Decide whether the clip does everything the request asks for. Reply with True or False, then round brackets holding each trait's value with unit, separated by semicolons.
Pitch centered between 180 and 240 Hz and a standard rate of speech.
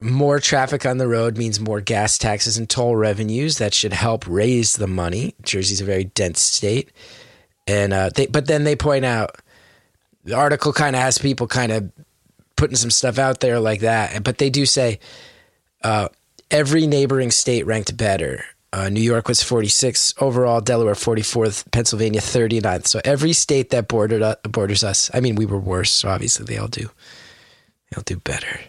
False (115 Hz; 180 wpm)